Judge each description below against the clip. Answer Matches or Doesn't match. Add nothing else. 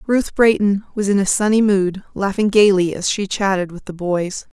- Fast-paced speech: Doesn't match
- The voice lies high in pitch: Matches